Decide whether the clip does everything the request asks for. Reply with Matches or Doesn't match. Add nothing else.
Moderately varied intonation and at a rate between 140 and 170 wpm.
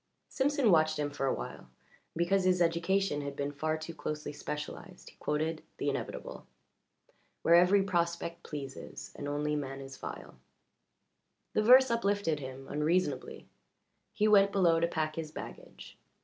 Matches